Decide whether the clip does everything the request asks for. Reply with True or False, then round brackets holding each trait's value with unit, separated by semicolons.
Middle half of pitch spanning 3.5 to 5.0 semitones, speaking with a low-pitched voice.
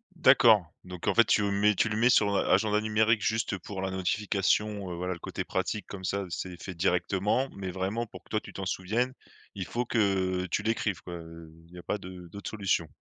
False (2.8 semitones; 100 Hz)